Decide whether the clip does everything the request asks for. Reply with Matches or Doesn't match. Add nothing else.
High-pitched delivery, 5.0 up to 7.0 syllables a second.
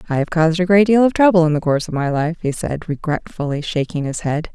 Doesn't match